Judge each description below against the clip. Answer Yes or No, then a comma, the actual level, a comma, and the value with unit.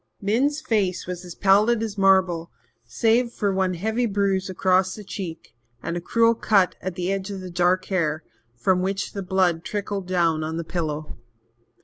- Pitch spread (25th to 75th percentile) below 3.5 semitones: Yes, narrow, 2.6 semitones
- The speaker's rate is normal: Yes, average, 175 wpm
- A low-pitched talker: No, high, 190 Hz